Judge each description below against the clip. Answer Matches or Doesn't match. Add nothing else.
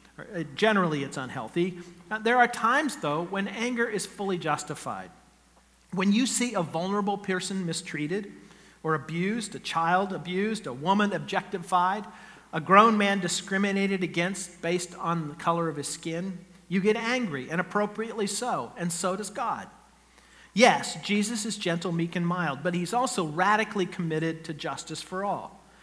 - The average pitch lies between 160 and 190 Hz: Matches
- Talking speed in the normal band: Matches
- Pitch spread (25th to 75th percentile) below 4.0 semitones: Matches